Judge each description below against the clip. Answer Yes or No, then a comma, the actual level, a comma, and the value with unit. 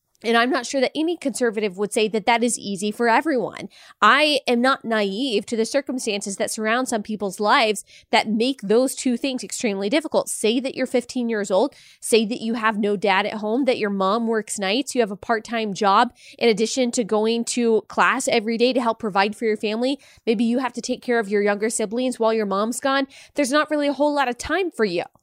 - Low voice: No, high, 230 Hz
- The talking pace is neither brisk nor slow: No, fast, 230 wpm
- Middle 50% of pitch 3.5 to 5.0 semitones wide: No, average, 3.0 semitones